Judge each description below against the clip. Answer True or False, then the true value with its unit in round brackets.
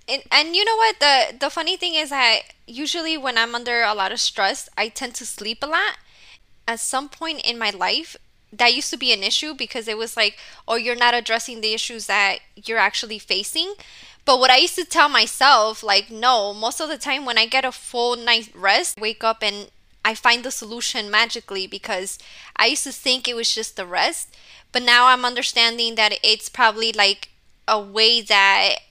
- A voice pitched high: True (235 Hz)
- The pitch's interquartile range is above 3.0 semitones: True (3.6 semitones)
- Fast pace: True (210 wpm)